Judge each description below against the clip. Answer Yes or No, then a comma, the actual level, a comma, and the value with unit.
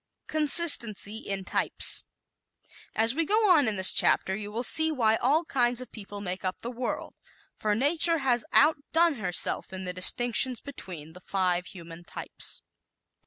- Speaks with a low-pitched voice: No, high, 230 Hz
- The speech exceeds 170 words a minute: No, average, 165 wpm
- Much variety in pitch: Yes, wide, 7.0 semitones